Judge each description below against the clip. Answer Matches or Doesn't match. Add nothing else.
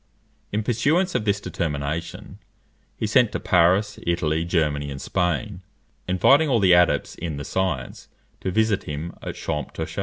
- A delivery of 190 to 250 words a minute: Doesn't match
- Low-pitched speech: Matches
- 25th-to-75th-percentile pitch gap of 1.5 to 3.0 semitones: Doesn't match